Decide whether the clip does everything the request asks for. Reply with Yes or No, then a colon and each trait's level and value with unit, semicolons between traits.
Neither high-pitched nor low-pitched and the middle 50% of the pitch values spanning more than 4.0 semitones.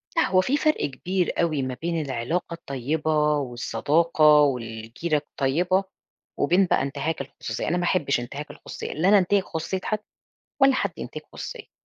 Yes: medium, 155 Hz; average, 4.7 semitones